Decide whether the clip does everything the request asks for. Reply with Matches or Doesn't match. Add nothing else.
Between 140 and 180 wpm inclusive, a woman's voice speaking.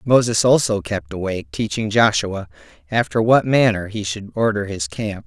Doesn't match